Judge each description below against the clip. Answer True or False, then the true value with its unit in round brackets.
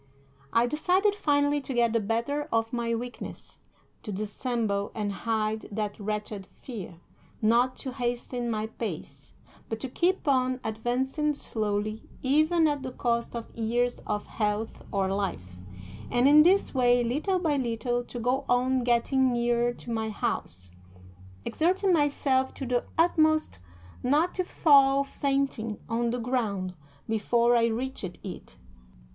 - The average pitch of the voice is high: True (240 Hz)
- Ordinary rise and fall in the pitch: True (3.7 semitones)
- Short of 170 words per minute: True (140 wpm)